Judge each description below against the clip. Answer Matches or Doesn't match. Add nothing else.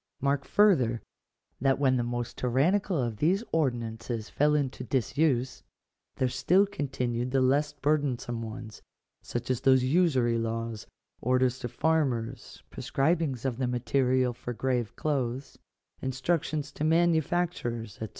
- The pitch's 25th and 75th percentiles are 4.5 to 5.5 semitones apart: Doesn't match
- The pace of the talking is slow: Matches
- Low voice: Matches